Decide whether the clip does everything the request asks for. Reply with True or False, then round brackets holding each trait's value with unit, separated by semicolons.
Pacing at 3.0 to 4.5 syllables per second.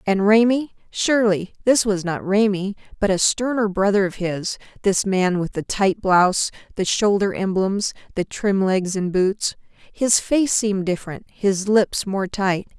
True (4.3 syllables/s)